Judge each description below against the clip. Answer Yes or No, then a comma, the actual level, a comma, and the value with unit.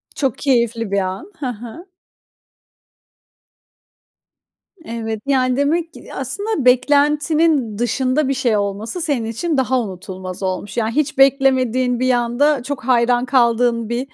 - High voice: Yes, very high, 250 Hz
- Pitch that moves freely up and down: No, average, 3.6 semitones